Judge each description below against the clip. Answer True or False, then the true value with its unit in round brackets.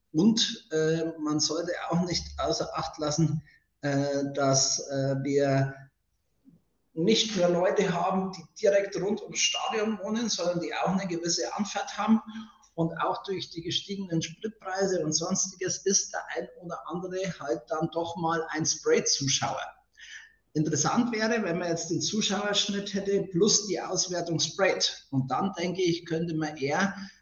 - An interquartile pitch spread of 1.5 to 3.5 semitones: False (4.1 semitones)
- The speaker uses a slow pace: False (150 wpm)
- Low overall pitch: False (170 Hz)